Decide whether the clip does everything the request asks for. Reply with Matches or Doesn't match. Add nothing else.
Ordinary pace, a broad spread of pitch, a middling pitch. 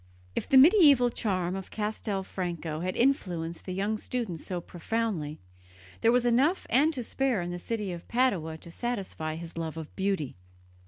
Doesn't match